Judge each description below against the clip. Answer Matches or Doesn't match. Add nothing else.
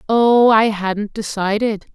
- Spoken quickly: Doesn't match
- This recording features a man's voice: Doesn't match